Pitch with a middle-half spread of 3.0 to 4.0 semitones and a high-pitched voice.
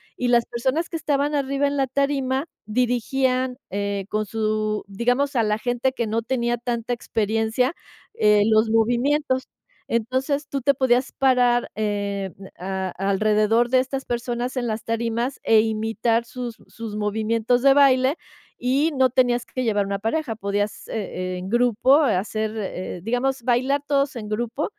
Yes: average, 3.3 semitones; high, 240 Hz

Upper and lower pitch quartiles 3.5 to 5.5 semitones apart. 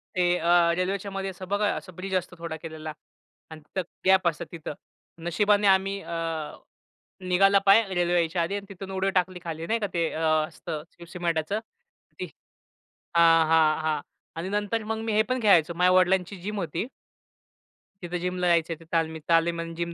No: average, 2.8 semitones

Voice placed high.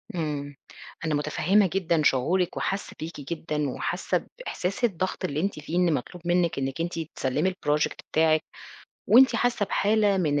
No: medium, 170 Hz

